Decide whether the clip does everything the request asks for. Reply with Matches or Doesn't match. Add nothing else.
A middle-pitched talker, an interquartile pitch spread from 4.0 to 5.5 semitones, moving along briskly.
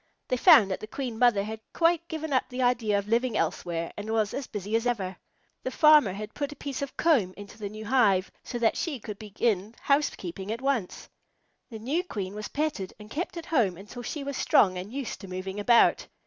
Doesn't match